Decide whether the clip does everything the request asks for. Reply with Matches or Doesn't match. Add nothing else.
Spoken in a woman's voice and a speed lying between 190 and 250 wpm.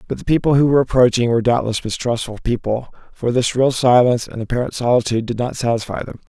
Doesn't match